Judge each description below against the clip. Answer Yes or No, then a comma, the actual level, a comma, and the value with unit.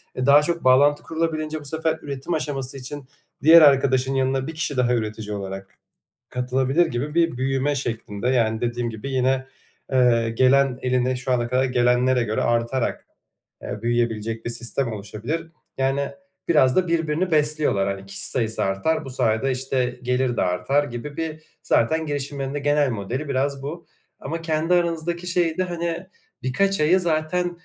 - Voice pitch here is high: No, low, 135 Hz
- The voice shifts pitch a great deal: No, average, 4.3 semitones